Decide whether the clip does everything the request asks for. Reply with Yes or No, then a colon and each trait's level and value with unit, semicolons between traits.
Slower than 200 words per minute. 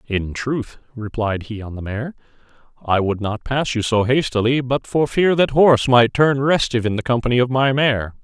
No: fast, 205 wpm